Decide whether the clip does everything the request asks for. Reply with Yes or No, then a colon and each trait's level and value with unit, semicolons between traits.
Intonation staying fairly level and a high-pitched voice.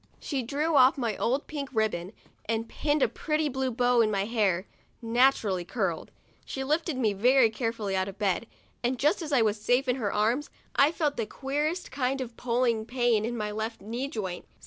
No: average, 3.9 semitones; high, 240 Hz